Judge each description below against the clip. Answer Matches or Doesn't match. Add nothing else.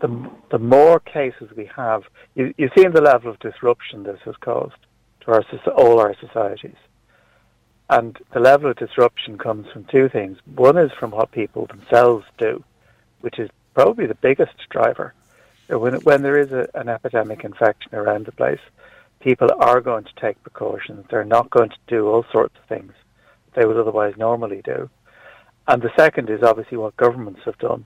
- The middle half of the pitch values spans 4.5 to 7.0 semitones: Matches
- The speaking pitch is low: Matches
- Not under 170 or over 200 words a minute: Matches